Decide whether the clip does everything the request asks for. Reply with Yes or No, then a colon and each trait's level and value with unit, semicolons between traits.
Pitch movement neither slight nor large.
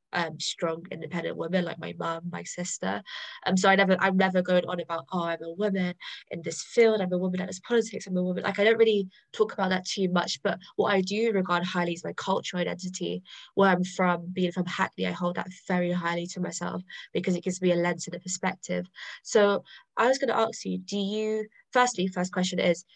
No: narrow, 2.0 semitones